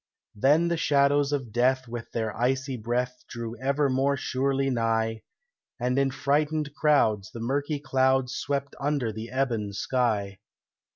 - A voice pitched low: Yes, low, 130 Hz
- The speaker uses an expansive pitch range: No, average, 3.2 semitones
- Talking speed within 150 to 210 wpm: No, average, 140 wpm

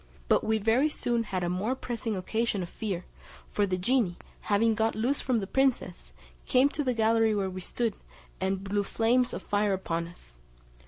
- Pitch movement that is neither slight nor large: Yes, average, 3.8 semitones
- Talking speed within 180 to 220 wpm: Yes, average, 190 wpm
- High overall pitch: Yes, high, 220 Hz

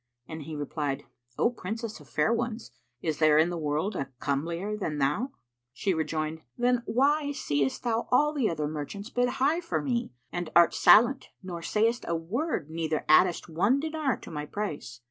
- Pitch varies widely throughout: Yes, wide, 7.7 semitones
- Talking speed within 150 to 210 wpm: Yes, average, 180 wpm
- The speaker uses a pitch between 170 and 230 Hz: Yes, medium, 185 Hz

